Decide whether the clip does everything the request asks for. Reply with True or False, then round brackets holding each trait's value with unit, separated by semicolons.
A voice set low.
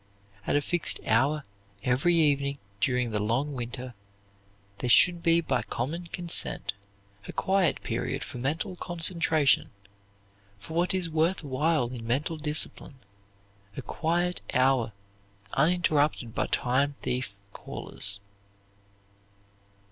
False (145 Hz)